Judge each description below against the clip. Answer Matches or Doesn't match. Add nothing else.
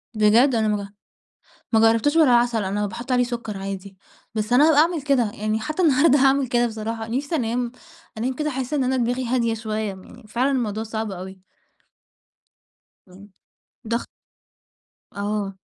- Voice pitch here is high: Matches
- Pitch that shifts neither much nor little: Matches